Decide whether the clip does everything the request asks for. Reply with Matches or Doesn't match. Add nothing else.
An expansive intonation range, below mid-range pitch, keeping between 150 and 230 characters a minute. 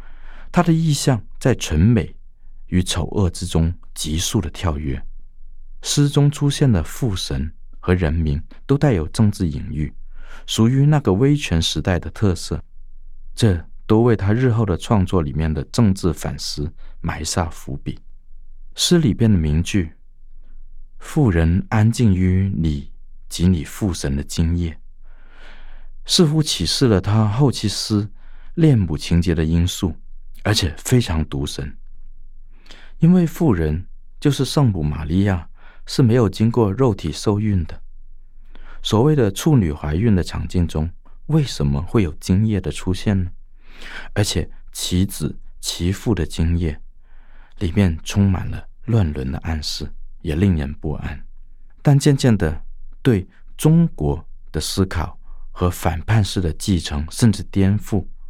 Matches